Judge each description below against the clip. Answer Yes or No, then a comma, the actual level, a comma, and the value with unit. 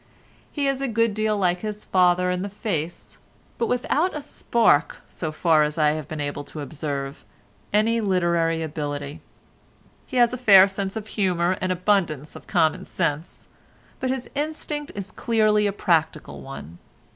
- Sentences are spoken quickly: No, average, 155 wpm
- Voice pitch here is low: No, medium, 185 Hz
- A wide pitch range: Yes, wide, 5.8 semitones